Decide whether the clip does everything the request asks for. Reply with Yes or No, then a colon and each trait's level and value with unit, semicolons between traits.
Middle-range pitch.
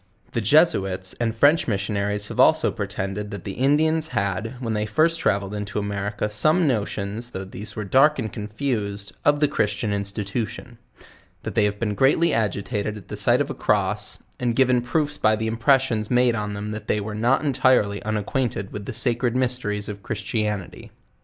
No: low, 110 Hz